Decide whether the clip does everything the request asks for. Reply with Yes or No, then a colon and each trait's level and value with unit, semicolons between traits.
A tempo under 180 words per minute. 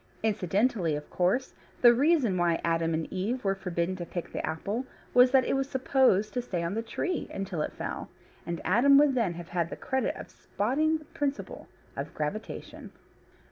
No: average, 185 wpm